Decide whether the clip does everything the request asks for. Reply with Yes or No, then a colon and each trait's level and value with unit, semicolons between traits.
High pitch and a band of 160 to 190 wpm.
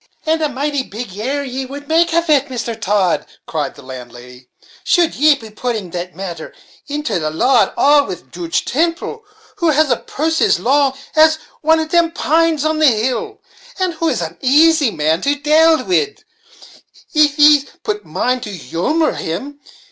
Yes: very high, 280 Hz; average, 180 wpm